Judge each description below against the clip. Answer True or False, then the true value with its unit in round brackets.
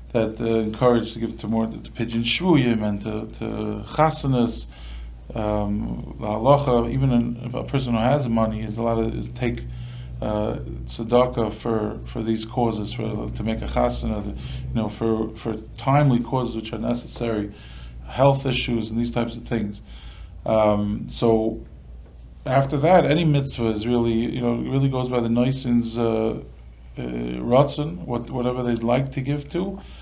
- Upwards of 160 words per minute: False (155 wpm)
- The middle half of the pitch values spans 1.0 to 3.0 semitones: True (2.6 semitones)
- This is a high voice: False (115 Hz)